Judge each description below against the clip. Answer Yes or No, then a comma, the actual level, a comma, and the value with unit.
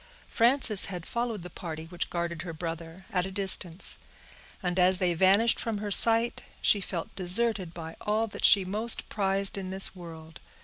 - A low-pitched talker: No, high, 190 Hz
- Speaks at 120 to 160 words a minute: No, average, 175 wpm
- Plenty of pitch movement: No, average, 3.4 semitones